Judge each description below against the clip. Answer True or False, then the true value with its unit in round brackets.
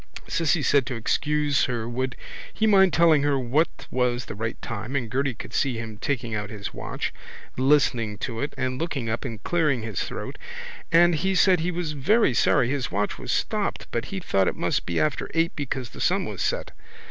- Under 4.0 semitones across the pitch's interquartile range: False (5.0 semitones)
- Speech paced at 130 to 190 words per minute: False (205 wpm)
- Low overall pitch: True (130 Hz)